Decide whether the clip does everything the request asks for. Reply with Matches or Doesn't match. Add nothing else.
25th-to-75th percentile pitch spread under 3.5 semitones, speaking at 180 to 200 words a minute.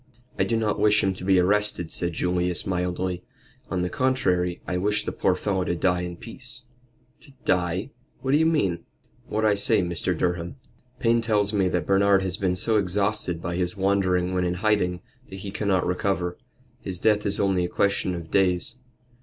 Matches